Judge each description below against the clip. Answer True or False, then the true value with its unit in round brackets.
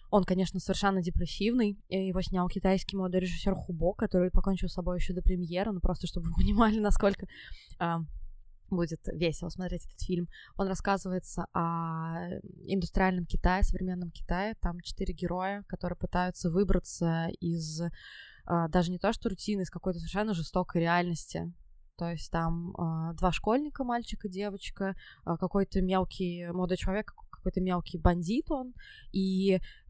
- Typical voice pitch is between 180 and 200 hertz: True (185 Hz)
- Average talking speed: True (145 wpm)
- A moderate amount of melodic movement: False (2.1 semitones)